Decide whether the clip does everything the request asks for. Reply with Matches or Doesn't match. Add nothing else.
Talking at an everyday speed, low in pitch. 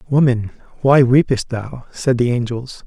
Matches